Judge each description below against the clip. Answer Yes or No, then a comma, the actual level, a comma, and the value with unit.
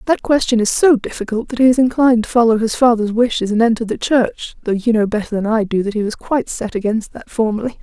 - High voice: Yes, high, 230 Hz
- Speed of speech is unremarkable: No, fast, 255 wpm